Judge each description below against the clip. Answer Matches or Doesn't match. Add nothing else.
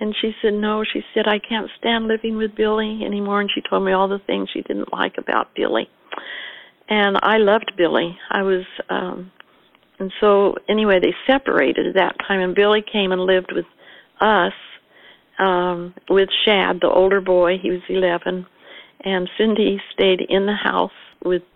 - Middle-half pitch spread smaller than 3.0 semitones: Matches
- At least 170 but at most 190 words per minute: Matches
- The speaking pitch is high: Matches